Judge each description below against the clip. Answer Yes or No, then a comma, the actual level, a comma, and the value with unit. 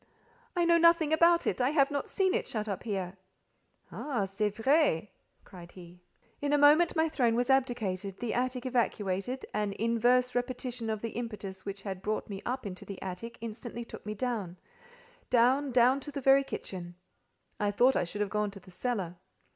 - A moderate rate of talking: Yes, average, 180 wpm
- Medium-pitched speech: No, high, 235 Hz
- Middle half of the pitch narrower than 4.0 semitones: No, average, 5.2 semitones